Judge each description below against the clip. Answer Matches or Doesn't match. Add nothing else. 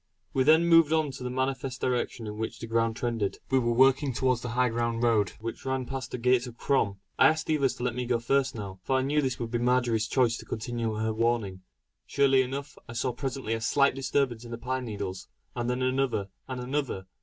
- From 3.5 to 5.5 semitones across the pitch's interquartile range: Doesn't match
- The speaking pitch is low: Matches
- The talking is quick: Matches